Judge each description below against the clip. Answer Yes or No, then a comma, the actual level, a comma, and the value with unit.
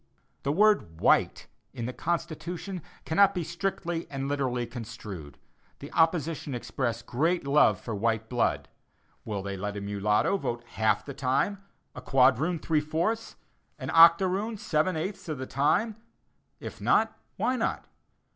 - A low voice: No, medium, 150 Hz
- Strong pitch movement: Yes, wide, 6.9 semitones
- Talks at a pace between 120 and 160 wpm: Yes, average, 145 wpm